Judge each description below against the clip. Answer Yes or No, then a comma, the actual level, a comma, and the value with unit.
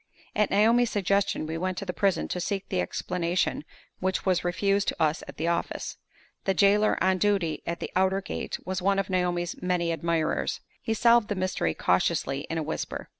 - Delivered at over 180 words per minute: Yes, average, 190 wpm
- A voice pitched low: No, medium, 185 Hz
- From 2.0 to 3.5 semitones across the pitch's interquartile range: Yes, average, 2.7 semitones